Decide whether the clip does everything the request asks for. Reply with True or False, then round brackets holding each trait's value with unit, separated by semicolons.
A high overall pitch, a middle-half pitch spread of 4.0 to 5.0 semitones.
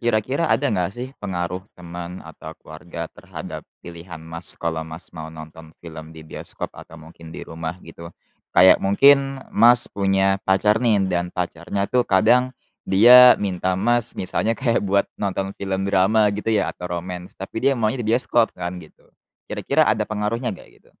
False (95 Hz; 4.5 semitones)